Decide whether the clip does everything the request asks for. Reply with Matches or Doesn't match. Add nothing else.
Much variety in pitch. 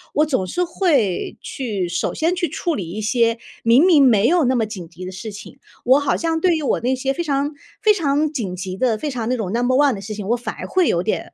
Matches